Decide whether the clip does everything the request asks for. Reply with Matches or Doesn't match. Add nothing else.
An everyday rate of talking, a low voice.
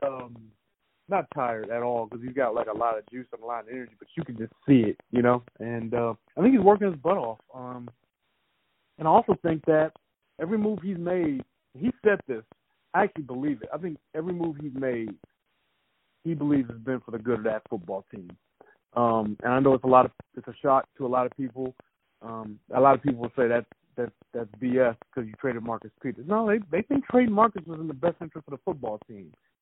Doesn't match